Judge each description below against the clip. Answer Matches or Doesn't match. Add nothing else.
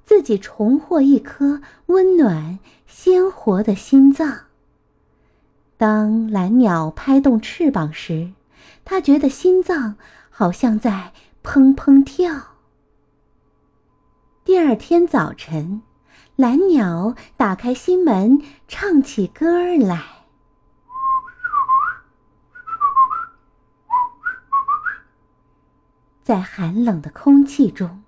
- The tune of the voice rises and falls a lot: Matches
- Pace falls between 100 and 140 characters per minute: Matches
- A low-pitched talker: Doesn't match